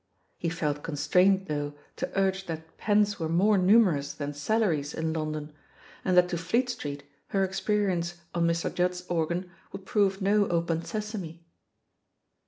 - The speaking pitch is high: No, medium, 175 Hz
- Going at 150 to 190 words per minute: Yes, average, 155 wpm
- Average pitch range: Yes, average, 3.4 semitones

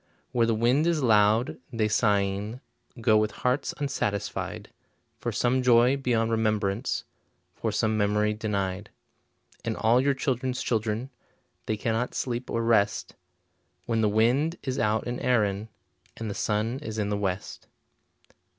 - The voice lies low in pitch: Yes, low, 110 Hz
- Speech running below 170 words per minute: Yes, average, 140 wpm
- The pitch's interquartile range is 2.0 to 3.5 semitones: Yes, average, 2.8 semitones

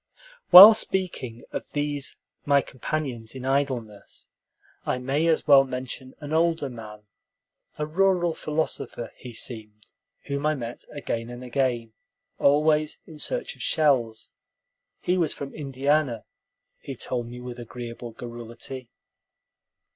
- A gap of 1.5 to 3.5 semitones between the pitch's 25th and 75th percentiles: No, average, 4.2 semitones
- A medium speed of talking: No, slow, 125 wpm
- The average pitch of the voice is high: No, low, 135 Hz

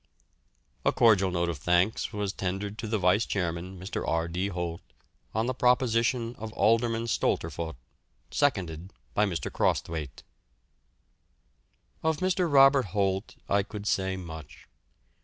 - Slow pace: Yes, slow, 130 wpm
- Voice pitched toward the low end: Yes, low, 100 Hz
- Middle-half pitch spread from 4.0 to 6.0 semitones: Yes, average, 4.7 semitones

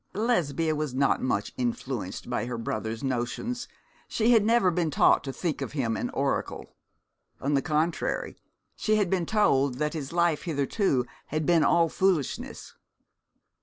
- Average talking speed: Yes, average, 150 wpm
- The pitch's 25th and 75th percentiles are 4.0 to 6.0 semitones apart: Yes, wide, 5.4 semitones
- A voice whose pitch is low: No, medium, 155 Hz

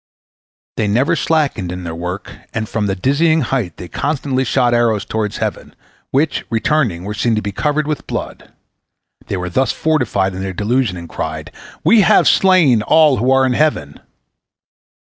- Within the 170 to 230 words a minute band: Yes, average, 175 wpm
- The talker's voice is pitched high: No, low, 120 Hz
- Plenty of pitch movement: Yes, wide, 7.0 semitones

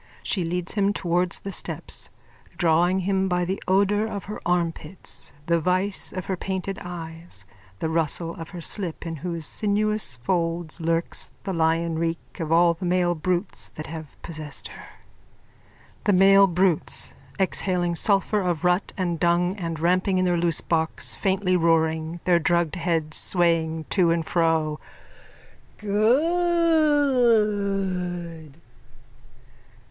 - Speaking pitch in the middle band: Yes, medium, 175 Hz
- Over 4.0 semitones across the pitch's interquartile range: No, average, 2.8 semitones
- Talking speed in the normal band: No, slow, 130 wpm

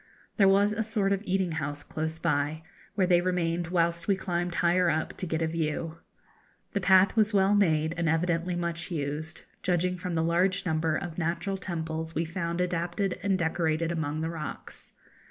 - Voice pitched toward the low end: No, medium, 170 Hz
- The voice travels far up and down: No, narrow, 2.4 semitones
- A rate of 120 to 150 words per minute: No, average, 180 wpm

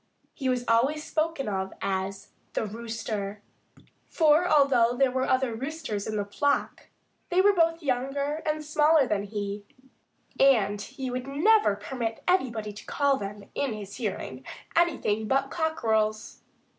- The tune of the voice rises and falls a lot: Yes, wide, 5.9 semitones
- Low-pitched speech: No, very high, 255 Hz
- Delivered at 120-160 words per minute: Yes, average, 145 wpm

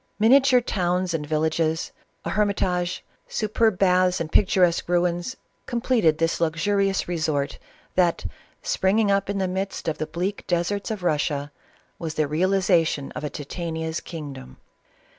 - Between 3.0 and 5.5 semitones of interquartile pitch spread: Yes, average, 3.6 semitones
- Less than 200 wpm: Yes, average, 140 wpm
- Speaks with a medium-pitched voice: Yes, medium, 180 Hz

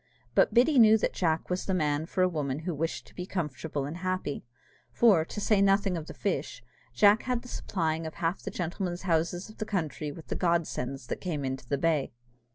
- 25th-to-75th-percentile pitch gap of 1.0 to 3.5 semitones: No, average, 4.1 semitones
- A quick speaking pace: Yes, fast, 215 wpm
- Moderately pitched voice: Yes, medium, 170 Hz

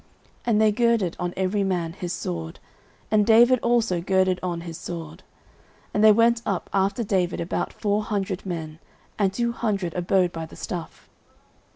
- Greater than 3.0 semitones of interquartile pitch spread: Yes, average, 3.6 semitones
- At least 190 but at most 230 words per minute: No, average, 165 wpm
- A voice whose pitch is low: No, high, 190 Hz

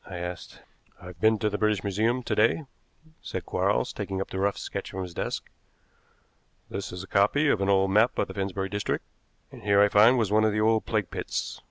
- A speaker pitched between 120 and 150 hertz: No, low, 100 Hz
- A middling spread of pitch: No, narrow, 2.1 semitones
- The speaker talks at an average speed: No, fast, 220 wpm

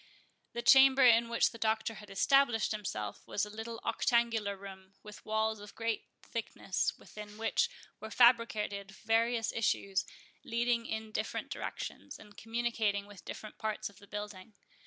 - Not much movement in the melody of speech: Yes, narrow, 2.1 semitones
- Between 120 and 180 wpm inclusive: Yes, average, 150 wpm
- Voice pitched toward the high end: Yes, high, 220 Hz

